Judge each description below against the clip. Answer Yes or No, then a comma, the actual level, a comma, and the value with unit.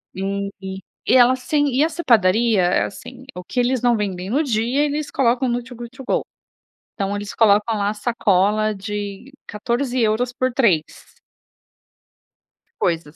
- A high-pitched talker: Yes, high, 225 Hz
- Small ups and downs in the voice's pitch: No, average, 4.1 semitones